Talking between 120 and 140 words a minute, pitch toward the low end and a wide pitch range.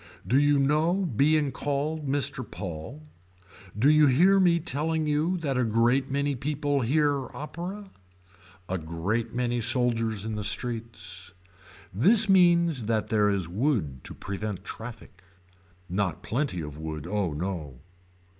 Yes: slow, 135 wpm; low, 125 Hz; wide, 6.9 semitones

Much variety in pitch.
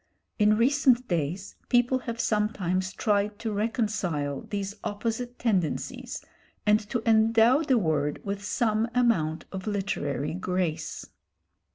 No: average, 4.0 semitones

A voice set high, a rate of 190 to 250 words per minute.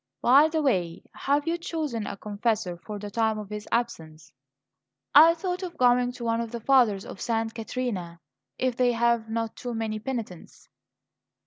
No: high, 230 Hz; average, 175 wpm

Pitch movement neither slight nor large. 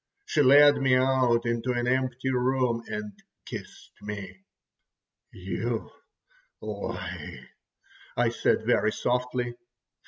No: narrow, 1.8 semitones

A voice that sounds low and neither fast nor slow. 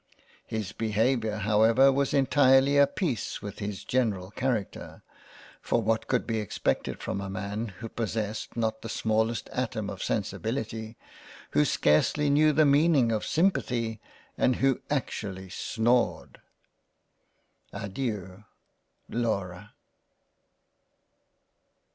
No: low, 115 Hz; slow, 115 wpm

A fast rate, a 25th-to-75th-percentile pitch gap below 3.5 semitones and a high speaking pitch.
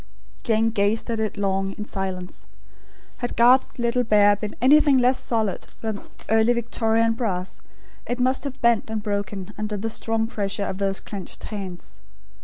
No: average, 160 wpm; average, 2.8 semitones; high, 220 Hz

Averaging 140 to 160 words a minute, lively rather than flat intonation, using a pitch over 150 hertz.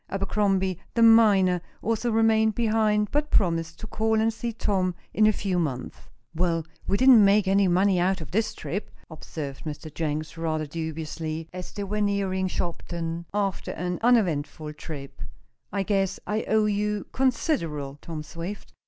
No: average, 155 wpm; average, 4.4 semitones; high, 190 Hz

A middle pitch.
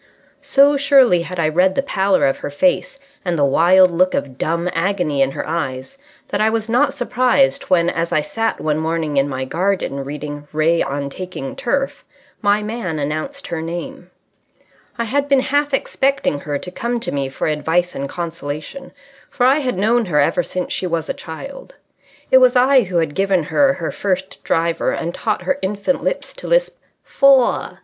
Yes: medium, 180 Hz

